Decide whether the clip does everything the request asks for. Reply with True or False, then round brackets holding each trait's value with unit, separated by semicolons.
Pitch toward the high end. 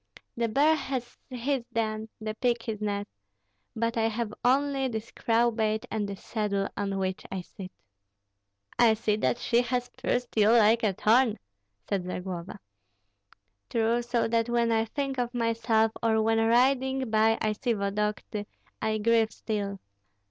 True (225 Hz)